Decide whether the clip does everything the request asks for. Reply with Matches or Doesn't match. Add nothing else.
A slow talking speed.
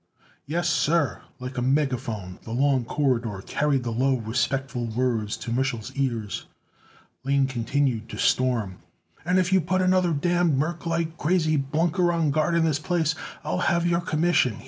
Doesn't match